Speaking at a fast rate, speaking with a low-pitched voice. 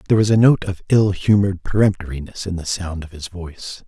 Yes: fast, 215 wpm; very low, 95 Hz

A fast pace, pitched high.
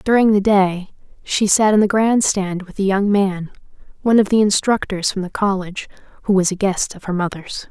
Yes: fast, 210 wpm; high, 200 Hz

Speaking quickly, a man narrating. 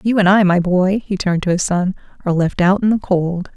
No: fast, 270 wpm; female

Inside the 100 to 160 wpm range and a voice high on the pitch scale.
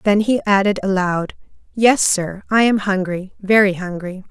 Yes: average, 140 wpm; high, 195 Hz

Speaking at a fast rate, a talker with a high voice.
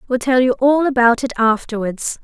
No: average, 190 wpm; high, 245 Hz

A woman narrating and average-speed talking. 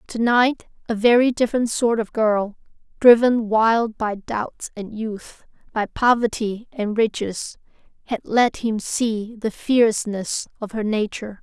No: female; slow, 130 wpm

